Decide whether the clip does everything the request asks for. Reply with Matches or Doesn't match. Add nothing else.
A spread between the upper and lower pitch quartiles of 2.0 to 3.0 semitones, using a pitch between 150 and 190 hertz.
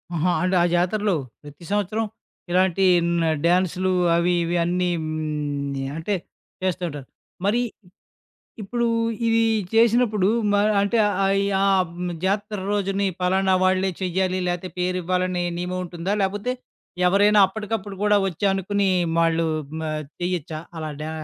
Matches